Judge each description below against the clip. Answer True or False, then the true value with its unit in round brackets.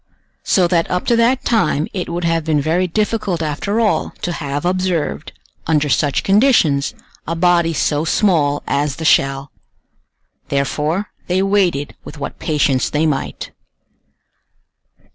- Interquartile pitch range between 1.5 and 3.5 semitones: False (4.1 semitones)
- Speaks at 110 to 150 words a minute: True (140 wpm)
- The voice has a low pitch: False (165 Hz)